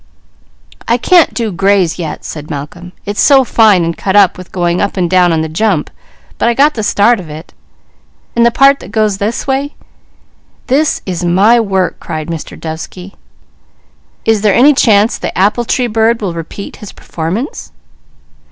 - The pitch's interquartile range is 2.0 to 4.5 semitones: No, average, 5.1 semitones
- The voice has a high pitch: Yes, high, 200 Hz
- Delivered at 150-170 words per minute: No, average, 180 wpm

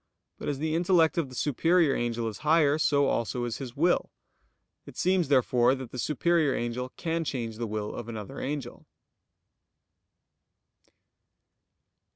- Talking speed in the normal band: Yes, average, 145 wpm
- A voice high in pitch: No, low, 135 Hz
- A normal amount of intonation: Yes, average, 5.0 semitones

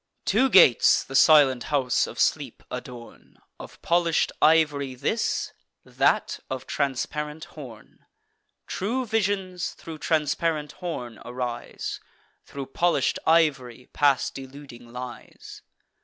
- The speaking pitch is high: No, medium, 145 Hz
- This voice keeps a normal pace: No, slow, 105 wpm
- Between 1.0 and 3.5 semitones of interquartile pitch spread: No, average, 4.4 semitones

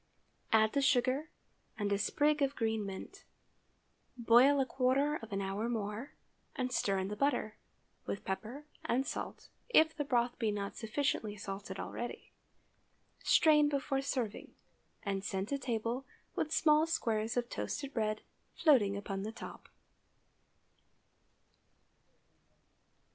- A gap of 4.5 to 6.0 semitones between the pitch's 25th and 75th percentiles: Yes, average, 5.1 semitones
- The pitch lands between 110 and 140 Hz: No, high, 240 Hz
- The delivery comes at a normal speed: No, slow, 130 wpm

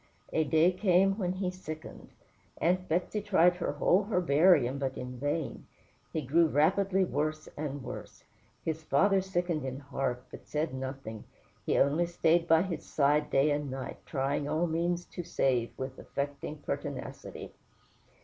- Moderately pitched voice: Yes, medium, 155 Hz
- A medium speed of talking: Yes, average, 150 wpm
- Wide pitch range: No, average, 4.1 semitones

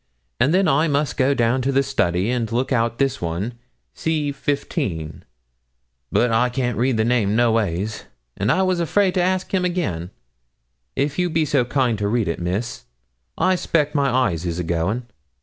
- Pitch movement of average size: No, wide, 5.8 semitones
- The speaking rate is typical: Yes, average, 185 wpm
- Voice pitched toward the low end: Yes, low, 125 Hz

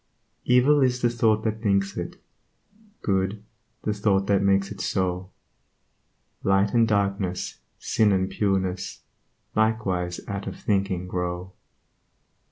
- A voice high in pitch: No, low, 100 Hz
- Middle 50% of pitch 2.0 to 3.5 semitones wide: Yes, narrow, 2.5 semitones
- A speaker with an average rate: No, slow, 120 wpm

